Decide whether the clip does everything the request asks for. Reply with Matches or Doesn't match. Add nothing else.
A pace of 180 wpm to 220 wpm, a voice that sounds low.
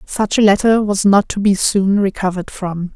Doesn't match